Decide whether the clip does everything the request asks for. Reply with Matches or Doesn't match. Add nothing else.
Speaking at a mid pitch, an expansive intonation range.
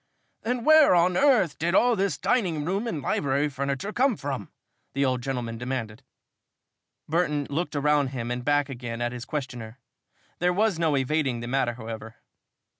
Matches